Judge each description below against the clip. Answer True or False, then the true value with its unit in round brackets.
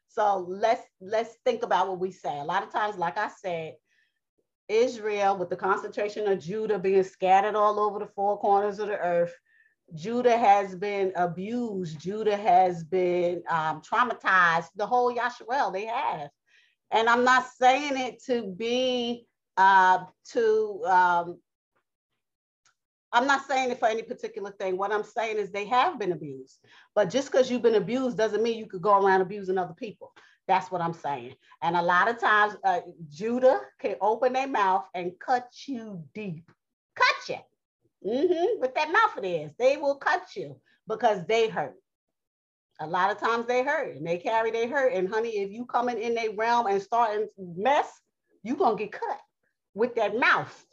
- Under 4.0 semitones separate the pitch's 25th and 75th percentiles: False (4.7 semitones)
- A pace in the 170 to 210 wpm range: True (175 wpm)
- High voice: True (215 Hz)